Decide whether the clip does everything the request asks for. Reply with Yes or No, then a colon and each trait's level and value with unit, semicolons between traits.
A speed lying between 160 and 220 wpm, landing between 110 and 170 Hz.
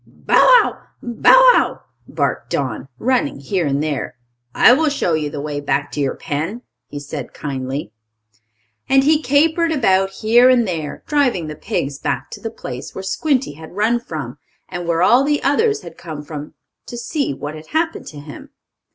No: average, 180 wpm; medium, 185 Hz